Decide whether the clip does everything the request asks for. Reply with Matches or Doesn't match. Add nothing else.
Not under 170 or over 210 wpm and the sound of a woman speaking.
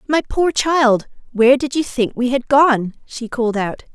Matches